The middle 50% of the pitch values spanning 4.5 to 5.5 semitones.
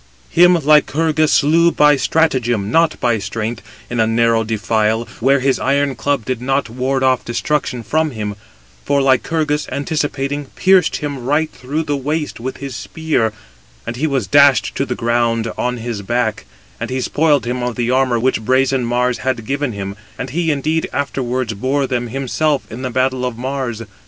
No: average, 3.5 semitones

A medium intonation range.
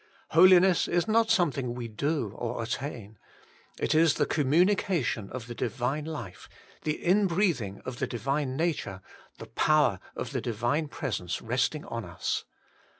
No: wide, 5.9 semitones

